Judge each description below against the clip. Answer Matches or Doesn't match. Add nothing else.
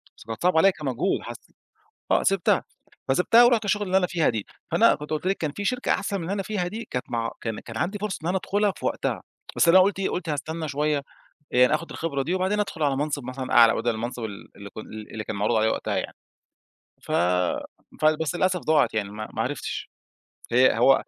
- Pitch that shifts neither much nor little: Doesn't match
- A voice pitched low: Doesn't match